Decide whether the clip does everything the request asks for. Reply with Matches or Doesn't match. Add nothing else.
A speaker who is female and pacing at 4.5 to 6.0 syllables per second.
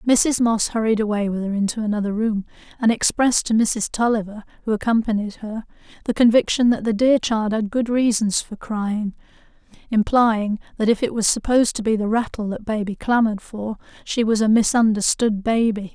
Matches